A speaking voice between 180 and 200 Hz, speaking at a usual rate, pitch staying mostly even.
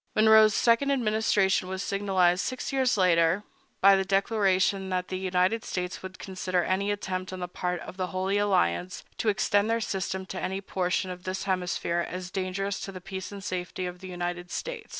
Yes: high, 190 Hz; average, 190 wpm; narrow, 1.8 semitones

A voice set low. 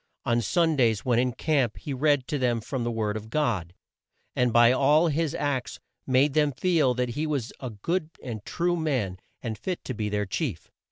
Yes: low, 130 Hz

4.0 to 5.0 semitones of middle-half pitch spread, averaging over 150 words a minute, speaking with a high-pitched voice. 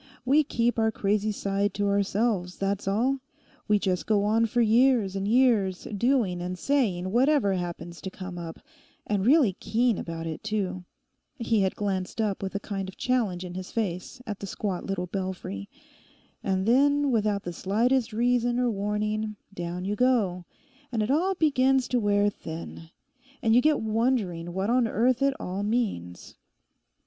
Yes: average, 4.4 semitones; average, 160 wpm; high, 210 Hz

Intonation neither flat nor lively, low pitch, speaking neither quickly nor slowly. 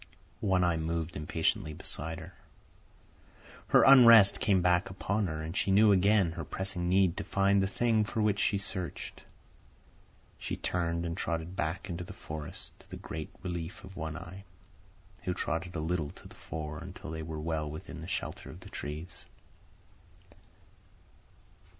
Yes: average, 3.2 semitones; very low, 90 Hz; average, 160 wpm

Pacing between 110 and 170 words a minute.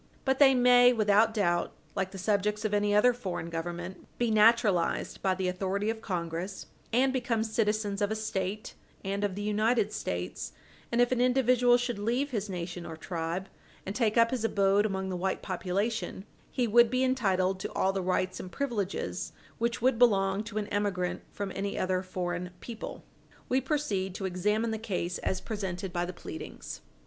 No: average, 180 wpm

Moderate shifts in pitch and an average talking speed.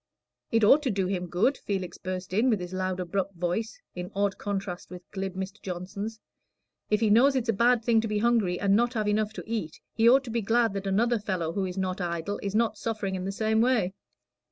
No: average, 3.3 semitones; fast, 230 wpm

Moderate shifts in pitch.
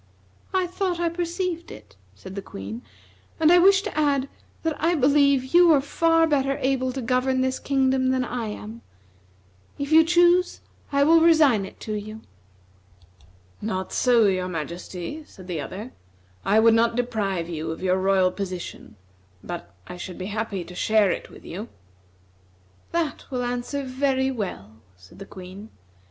No: wide, 7.4 semitones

